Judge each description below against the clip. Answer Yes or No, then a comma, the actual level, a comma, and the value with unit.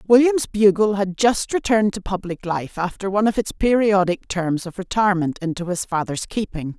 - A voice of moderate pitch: No, high, 195 Hz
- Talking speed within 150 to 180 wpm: Yes, average, 175 wpm